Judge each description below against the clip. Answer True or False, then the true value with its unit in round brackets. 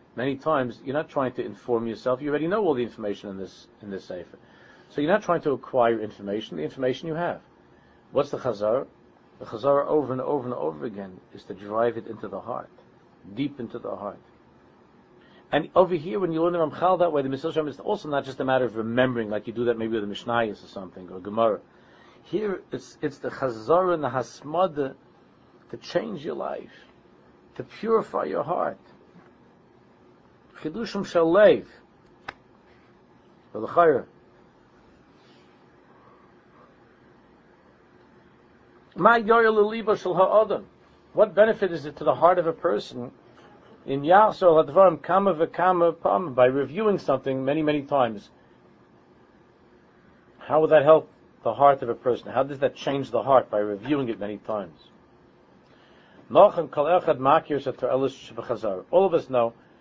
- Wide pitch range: True (6.3 semitones)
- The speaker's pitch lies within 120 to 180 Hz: True (140 Hz)